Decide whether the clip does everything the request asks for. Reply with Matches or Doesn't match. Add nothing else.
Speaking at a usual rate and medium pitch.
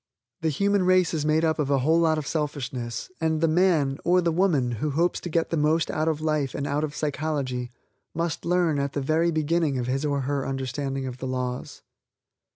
Doesn't match